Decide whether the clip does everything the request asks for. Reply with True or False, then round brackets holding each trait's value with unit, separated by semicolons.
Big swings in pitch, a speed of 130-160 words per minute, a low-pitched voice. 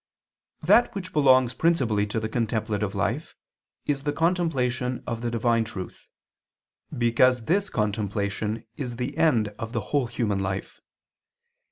False (4.1 semitones; 135 wpm; 120 Hz)